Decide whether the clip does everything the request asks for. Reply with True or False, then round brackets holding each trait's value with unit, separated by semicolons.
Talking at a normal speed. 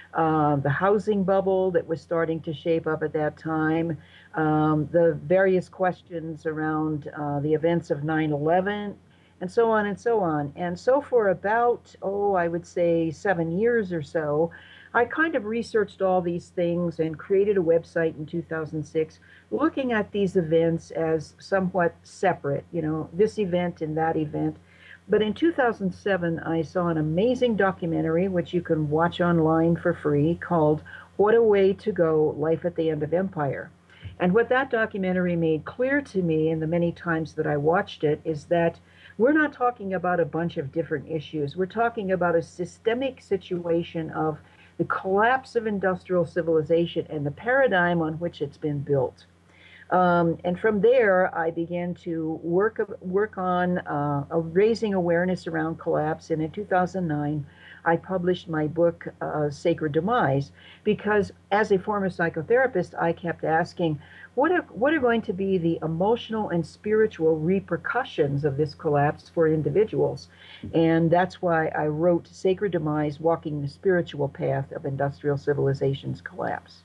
True (160 wpm)